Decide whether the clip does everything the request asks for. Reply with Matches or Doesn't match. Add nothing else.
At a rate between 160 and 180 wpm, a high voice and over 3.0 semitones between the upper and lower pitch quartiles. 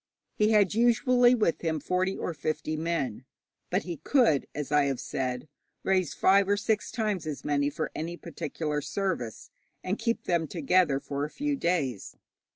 Doesn't match